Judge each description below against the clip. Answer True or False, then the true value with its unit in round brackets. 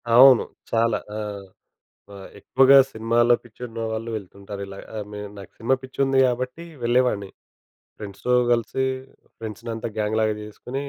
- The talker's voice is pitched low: True (115 Hz)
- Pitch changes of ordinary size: True (3.0 semitones)